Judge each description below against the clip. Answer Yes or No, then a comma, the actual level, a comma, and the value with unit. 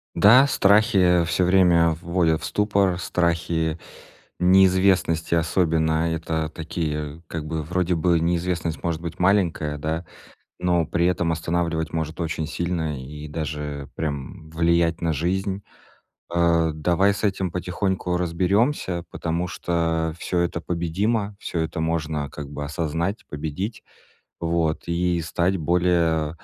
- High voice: No, very low, 85 Hz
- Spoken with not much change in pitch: Yes, narrow, 2.0 semitones